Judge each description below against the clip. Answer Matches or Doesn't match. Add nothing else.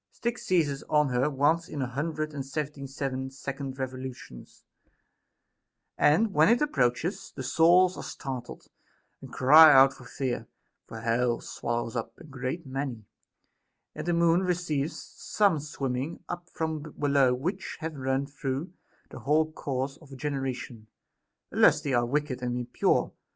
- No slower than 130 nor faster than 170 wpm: Matches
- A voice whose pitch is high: Doesn't match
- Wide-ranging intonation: Doesn't match